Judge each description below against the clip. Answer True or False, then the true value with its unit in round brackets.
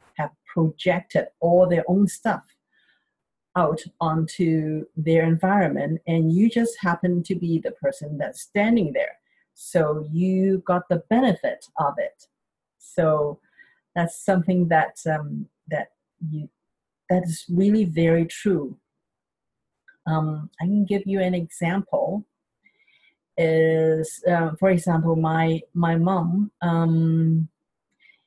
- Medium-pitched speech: True (170 Hz)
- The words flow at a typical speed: False (120 wpm)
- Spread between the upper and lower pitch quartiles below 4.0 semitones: True (3.0 semitones)